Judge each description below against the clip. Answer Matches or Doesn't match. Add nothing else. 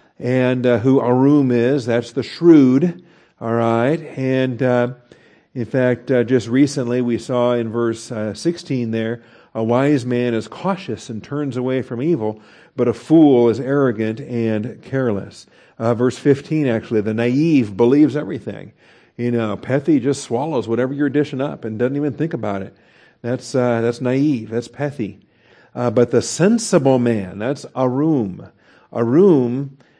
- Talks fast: Doesn't match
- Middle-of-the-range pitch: Doesn't match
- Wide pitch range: Doesn't match